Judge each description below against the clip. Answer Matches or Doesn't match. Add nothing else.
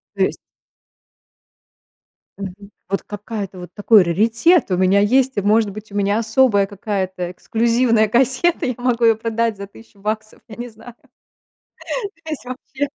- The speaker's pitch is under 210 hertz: Doesn't match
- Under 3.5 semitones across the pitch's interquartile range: Matches